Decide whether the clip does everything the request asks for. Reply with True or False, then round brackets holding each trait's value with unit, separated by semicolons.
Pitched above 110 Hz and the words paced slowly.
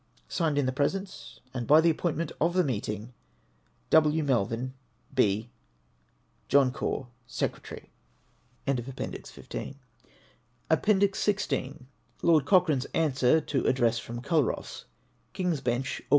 True (140 Hz; 120 wpm)